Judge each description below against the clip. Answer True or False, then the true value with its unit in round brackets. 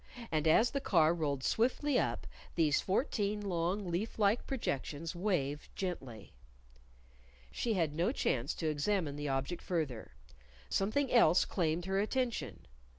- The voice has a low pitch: False (175 Hz)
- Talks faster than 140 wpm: False (135 wpm)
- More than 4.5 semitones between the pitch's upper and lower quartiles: True (5.6 semitones)